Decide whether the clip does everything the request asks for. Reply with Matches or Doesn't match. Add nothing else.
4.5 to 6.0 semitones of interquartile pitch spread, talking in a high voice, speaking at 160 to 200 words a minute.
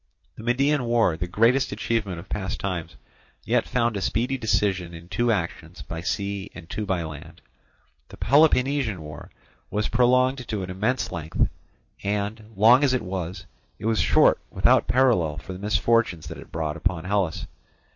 Doesn't match